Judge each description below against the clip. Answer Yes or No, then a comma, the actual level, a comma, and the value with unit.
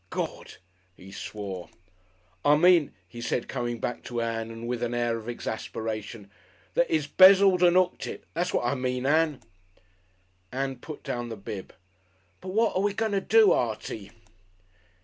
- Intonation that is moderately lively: No, wide, 7.4 semitones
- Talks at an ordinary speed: Yes, average, 165 wpm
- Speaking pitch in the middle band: No, low, 125 Hz